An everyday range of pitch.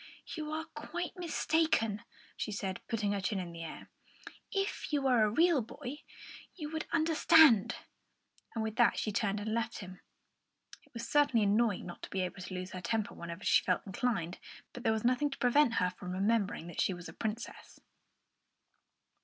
No: wide, 7.2 semitones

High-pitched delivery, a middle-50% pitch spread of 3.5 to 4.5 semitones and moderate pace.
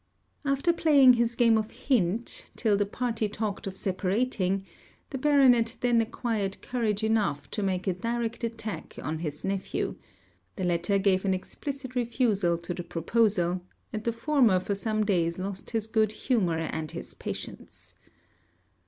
Yes: high, 215 Hz; average, 4.0 semitones; average, 155 wpm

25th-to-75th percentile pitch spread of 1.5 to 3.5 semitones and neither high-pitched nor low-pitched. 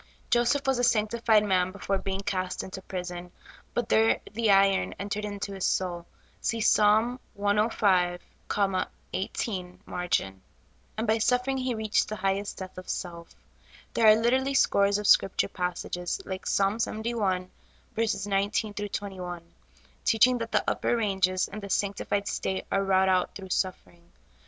No: average, 2.8 semitones; high, 200 Hz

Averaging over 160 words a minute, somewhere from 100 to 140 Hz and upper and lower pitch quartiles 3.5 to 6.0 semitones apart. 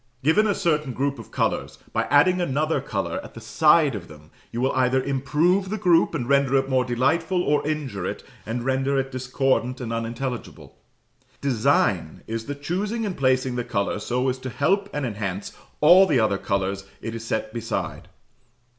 Yes: average, 180 wpm; low, 135 Hz; average, 4.3 semitones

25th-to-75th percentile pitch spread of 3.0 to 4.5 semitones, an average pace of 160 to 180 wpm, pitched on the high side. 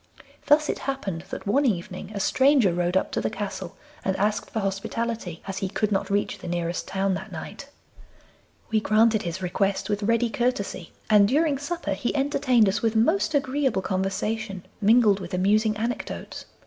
Yes: average, 4.0 semitones; average, 175 wpm; high, 210 Hz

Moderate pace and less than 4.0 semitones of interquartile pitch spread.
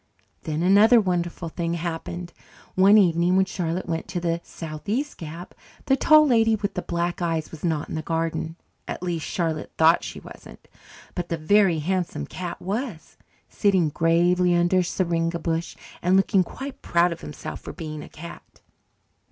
Yes: average, 170 wpm; narrow, 2.4 semitones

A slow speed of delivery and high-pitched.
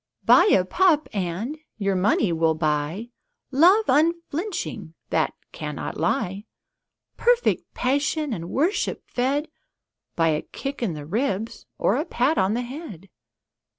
Yes: slow, 130 wpm; high, 240 Hz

